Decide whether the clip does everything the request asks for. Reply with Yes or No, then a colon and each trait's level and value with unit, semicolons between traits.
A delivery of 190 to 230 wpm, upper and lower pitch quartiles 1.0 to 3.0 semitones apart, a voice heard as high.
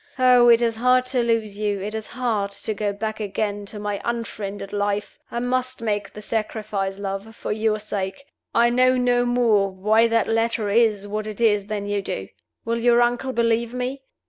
Yes: average, 195 wpm; average, 2.7 semitones; high, 220 Hz